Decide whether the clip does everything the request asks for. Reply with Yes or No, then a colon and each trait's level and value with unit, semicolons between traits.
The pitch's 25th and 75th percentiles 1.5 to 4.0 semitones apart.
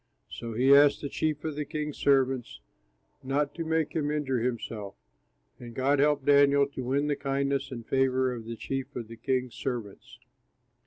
Yes: narrow, 2.6 semitones